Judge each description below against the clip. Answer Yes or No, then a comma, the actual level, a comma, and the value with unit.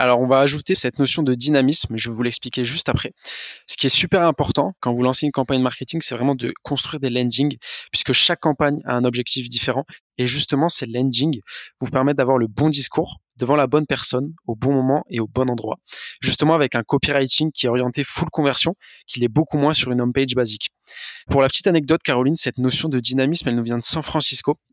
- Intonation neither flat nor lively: Yes, average, 3.1 semitones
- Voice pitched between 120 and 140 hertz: Yes, low, 135 Hz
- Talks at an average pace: No, fast, 225 wpm